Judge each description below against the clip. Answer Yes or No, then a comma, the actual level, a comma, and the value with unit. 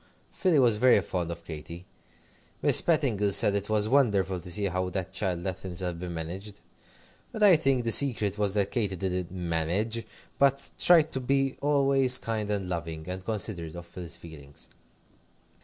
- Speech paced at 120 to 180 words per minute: Yes, average, 170 wpm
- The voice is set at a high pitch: No, low, 100 Hz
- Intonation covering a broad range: Yes, wide, 5.9 semitones